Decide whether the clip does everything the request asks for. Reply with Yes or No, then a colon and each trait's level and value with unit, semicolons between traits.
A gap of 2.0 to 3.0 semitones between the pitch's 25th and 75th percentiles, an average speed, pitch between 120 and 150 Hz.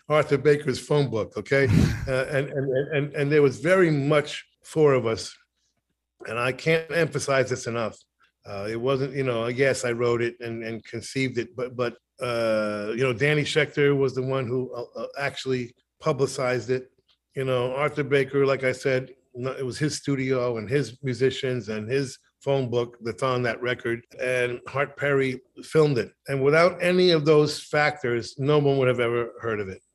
Yes: average, 2.7 semitones; average, 185 wpm; low, 130 Hz